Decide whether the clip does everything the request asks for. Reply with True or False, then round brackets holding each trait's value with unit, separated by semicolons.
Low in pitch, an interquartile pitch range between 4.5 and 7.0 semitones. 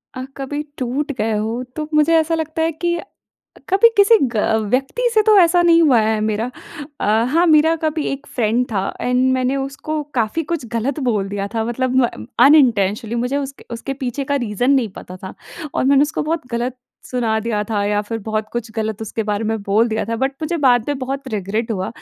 False (250 Hz; 5.2 semitones)